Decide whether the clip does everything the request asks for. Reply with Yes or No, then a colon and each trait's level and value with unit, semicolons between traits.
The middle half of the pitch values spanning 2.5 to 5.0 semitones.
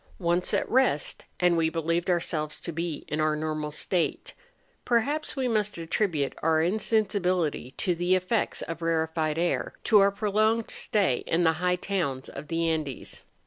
Yes: average, 3.9 semitones